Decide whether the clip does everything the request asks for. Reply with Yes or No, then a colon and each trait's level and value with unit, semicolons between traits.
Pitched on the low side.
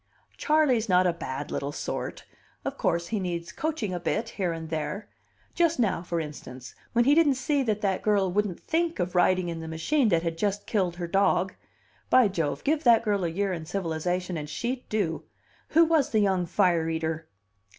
No: medium, 185 Hz